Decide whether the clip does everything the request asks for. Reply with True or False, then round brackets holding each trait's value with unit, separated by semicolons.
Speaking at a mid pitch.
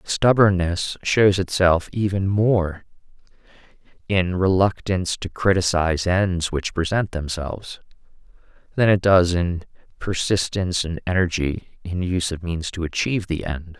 False (90 Hz)